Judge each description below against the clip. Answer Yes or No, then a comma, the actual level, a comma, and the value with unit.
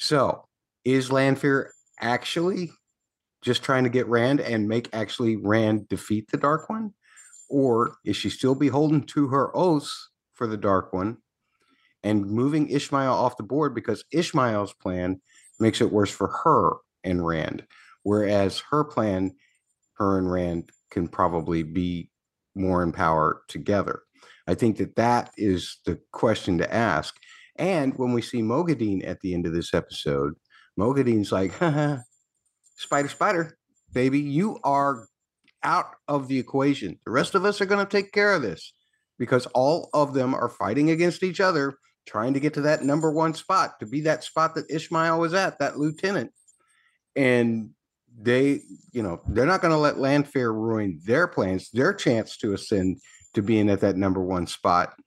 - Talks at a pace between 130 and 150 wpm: No, average, 165 wpm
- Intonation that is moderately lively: No, wide, 6.6 semitones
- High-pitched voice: No, low, 125 Hz